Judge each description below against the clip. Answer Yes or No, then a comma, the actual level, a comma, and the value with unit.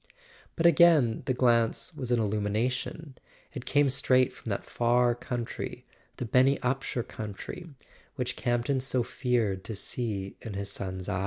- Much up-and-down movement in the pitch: No, average, 3.0 semitones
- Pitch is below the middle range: Yes, low, 120 Hz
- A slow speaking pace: No, average, 155 wpm